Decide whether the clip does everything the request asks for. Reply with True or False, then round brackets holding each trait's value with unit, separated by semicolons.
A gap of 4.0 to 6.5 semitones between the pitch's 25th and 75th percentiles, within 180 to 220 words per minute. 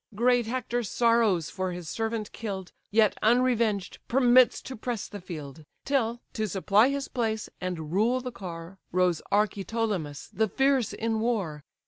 False (4.5 semitones; 145 wpm)